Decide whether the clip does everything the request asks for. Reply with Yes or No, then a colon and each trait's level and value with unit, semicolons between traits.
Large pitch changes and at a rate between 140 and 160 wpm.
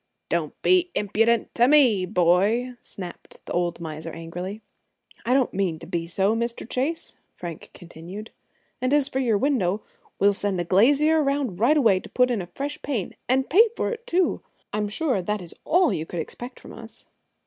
No: wide, 6.8 semitones; average, 190 wpm